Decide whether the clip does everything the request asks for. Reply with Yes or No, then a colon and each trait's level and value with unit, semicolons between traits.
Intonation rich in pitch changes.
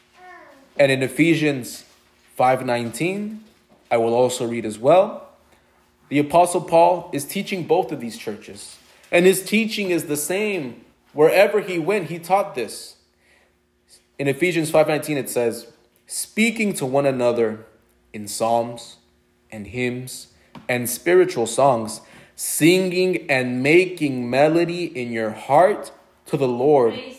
Yes: wide, 7.4 semitones